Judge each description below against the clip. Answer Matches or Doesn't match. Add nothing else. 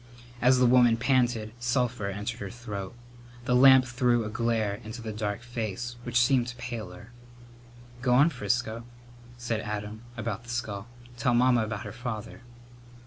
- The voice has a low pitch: Matches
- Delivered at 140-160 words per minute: Matches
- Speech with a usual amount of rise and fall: Doesn't match